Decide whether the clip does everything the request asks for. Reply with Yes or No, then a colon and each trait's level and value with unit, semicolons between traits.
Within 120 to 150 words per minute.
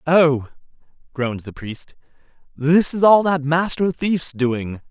Yes: slow, 135 wpm